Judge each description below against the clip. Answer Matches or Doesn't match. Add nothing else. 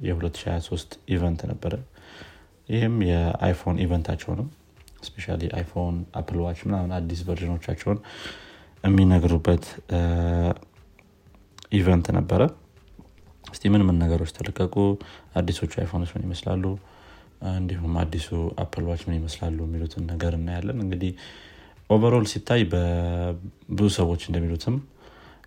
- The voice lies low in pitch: Matches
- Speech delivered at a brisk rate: Doesn't match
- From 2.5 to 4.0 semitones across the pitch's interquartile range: Matches